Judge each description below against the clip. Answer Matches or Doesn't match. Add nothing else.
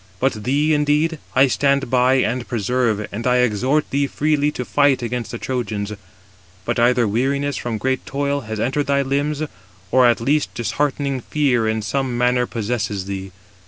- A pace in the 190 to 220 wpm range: Doesn't match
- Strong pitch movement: Doesn't match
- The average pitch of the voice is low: Matches